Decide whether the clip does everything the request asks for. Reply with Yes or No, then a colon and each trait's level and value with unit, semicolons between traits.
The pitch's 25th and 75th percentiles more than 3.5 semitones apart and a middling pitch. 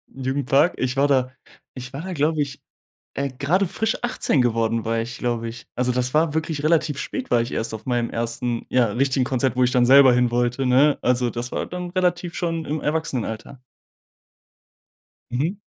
No: average, 4.0 semitones; low, 130 Hz